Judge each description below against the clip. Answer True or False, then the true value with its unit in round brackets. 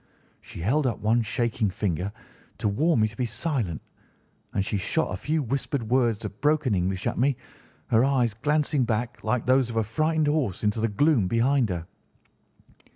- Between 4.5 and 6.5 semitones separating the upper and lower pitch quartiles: True (4.9 semitones)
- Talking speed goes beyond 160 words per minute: True (180 wpm)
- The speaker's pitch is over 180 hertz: False (115 Hz)